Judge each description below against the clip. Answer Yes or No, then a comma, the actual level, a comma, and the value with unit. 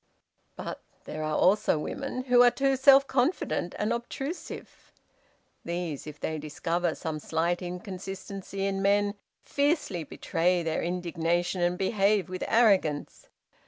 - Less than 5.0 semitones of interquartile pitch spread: No, average, 5.3 semitones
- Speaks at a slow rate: Yes, slow, 130 wpm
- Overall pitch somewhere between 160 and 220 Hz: Yes, medium, 185 Hz